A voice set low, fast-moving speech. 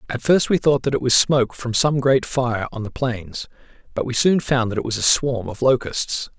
Yes: low, 125 Hz; fast, 245 wpm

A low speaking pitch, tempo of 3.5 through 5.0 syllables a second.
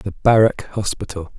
Yes: low, 100 Hz; 4.6 syllables/s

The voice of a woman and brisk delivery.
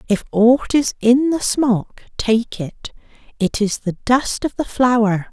No: female; average, 170 wpm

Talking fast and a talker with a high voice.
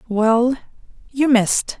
No: slow, 100 wpm; high, 240 Hz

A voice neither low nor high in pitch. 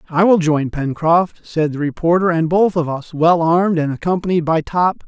Yes: medium, 165 Hz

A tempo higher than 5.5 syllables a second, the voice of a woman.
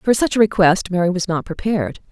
Yes: 6.0 syllables/s; female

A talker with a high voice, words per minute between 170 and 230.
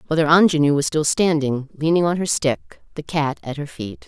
No: medium, 150 Hz; fast, 205 wpm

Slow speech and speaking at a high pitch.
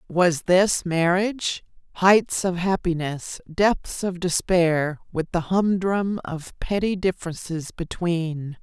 No: slow, 105 wpm; medium, 180 Hz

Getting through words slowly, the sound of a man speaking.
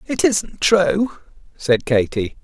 Yes: slow, 125 wpm; male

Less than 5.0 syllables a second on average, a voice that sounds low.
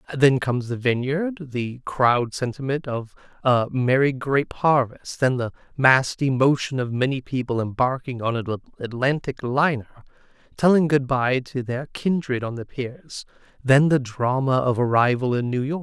Yes: 4.5 syllables/s; low, 130 Hz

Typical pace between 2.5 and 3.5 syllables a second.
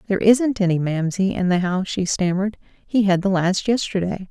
No: 5.5 syllables/s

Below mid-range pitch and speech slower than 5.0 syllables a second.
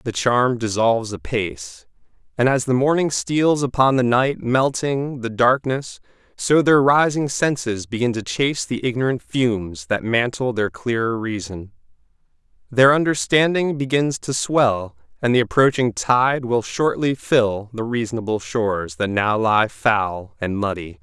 Yes: low, 120 Hz; 4.3 syllables/s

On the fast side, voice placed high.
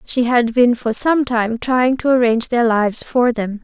Yes: fast, 215 wpm; high, 240 Hz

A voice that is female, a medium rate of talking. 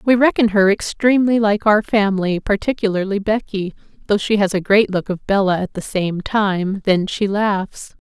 Yes: female; average, 180 wpm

